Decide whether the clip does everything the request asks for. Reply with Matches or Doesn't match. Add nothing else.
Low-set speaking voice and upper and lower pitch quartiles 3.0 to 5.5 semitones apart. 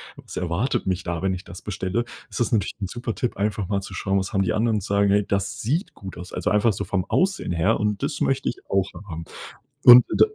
Matches